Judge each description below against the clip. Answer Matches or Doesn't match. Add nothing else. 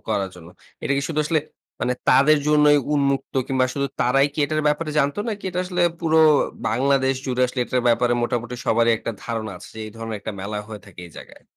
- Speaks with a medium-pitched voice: Doesn't match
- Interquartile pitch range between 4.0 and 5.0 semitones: Matches